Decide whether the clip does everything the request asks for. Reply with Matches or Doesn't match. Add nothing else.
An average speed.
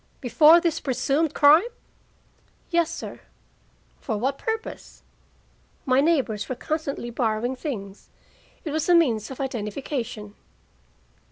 Doesn't match